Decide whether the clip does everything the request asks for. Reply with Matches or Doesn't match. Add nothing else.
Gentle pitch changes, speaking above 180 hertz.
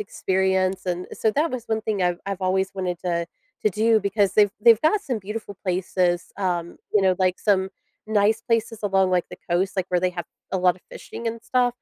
Doesn't match